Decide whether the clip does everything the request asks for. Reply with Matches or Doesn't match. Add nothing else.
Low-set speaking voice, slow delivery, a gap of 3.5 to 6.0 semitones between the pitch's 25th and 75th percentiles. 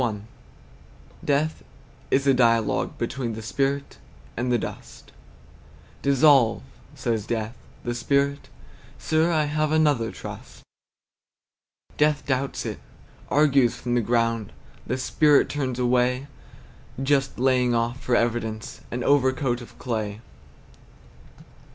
Doesn't match